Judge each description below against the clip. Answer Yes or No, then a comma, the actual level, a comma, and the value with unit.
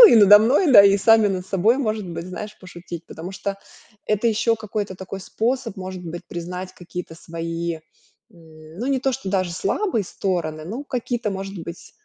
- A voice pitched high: Yes, high, 195 Hz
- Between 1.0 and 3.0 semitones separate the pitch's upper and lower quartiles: No, average, 4.1 semitones